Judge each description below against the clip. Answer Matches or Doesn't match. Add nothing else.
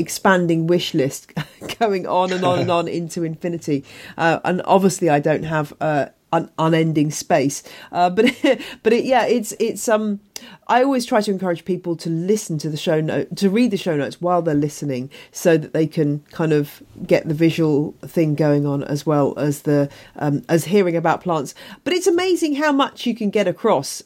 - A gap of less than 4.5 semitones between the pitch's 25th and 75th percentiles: Doesn't match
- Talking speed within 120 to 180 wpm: Doesn't match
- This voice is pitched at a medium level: Matches